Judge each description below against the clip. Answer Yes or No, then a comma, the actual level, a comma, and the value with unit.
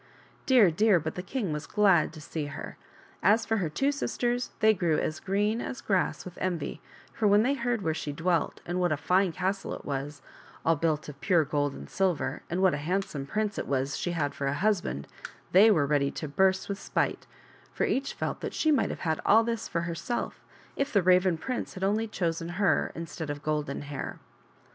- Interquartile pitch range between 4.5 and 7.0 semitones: Yes, average, 5.3 semitones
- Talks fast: Yes, fast, 215 wpm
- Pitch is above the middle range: No, medium, 180 Hz